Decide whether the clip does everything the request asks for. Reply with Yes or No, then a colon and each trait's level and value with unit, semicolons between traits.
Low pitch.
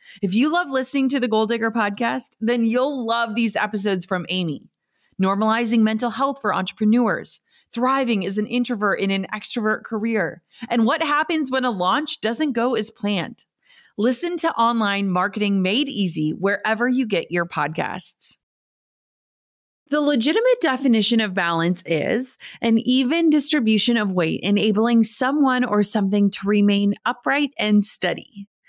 No: high, 225 Hz